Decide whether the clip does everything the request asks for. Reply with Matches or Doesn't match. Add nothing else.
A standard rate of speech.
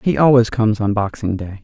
Doesn't match